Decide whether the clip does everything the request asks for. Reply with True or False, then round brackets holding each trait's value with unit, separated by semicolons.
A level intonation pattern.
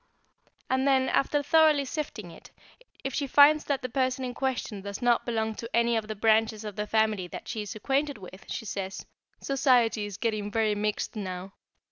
False (4.2 semitones)